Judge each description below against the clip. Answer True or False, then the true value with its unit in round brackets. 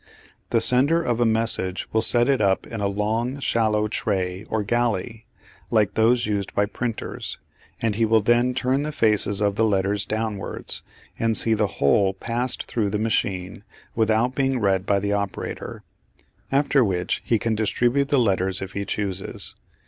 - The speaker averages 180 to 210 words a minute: False (170 wpm)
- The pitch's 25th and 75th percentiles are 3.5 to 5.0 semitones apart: False (3.0 semitones)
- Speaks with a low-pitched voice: True (110 Hz)